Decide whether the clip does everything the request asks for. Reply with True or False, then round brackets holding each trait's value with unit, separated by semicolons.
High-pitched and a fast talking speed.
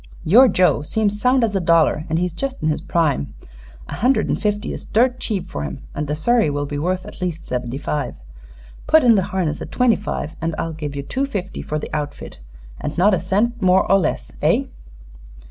False (180 Hz; 215 wpm)